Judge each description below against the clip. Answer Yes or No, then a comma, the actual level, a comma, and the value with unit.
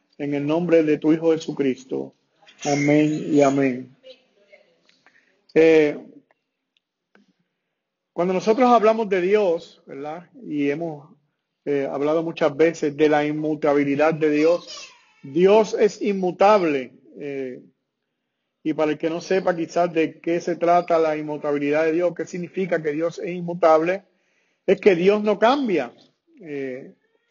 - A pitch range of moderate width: Yes, average, 3.6 semitones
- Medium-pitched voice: Yes, medium, 160 Hz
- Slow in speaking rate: Yes, slow, 130 wpm